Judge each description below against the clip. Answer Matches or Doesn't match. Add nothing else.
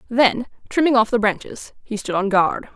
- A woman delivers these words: Matches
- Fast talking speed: Doesn't match